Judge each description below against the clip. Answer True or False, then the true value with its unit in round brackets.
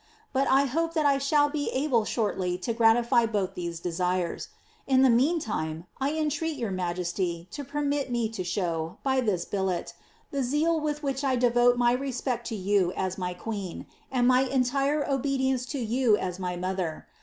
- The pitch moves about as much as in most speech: False (6.7 semitones)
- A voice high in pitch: True (240 Hz)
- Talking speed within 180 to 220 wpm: True (185 wpm)